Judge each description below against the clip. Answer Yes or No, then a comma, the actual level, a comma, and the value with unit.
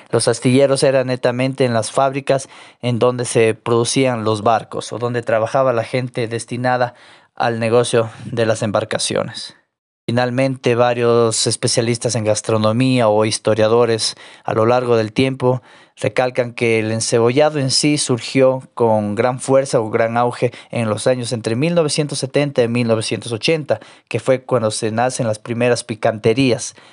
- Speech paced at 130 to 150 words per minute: Yes, average, 145 wpm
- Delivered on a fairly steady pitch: Yes, narrow, 2.2 semitones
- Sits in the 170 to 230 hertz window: No, low, 120 Hz